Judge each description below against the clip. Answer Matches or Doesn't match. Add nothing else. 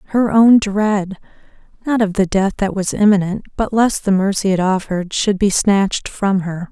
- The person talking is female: Matches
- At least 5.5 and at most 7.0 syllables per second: Doesn't match